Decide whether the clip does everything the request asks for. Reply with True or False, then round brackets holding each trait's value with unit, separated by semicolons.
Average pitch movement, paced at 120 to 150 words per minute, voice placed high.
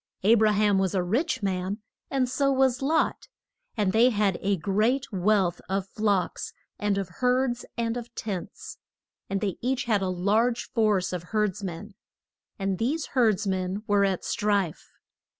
False (3.6 semitones; 165 wpm; 205 Hz)